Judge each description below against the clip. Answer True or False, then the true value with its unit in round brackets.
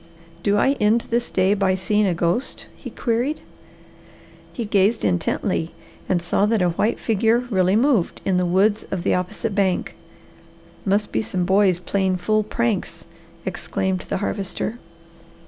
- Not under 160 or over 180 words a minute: False (150 wpm)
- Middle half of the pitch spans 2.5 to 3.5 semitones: True (3.0 semitones)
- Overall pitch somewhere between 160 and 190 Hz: False (200 Hz)